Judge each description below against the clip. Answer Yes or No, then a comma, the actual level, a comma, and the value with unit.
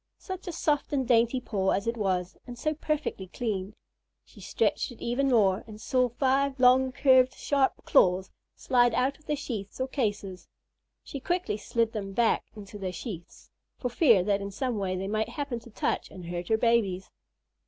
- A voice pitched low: No, high, 235 Hz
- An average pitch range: Yes, average, 4.9 semitones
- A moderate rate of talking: Yes, average, 185 wpm